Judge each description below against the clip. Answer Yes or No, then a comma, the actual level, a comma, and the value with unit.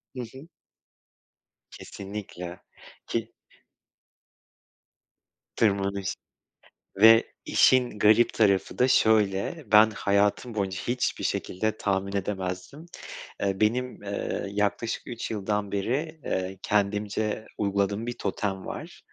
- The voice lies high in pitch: No, low, 105 Hz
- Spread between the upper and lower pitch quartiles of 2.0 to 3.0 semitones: Yes, narrow, 2.4 semitones